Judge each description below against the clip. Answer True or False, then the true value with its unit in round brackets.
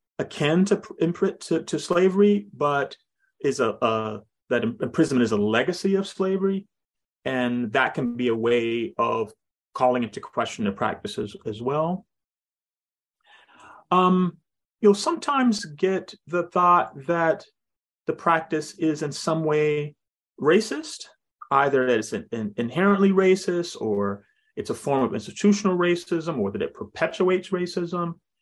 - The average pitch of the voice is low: False (170 Hz)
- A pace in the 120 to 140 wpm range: True (135 wpm)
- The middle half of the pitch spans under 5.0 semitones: False (5.6 semitones)